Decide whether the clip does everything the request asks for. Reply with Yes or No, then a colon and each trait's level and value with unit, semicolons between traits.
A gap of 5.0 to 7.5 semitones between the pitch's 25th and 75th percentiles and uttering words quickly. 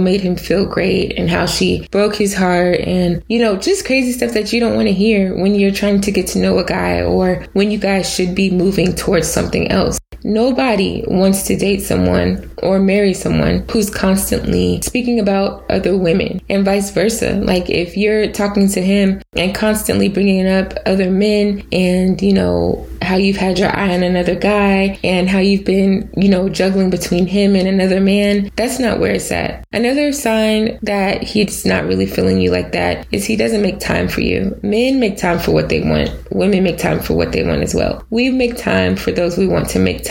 No: narrow, 2.6 semitones; fast, 210 wpm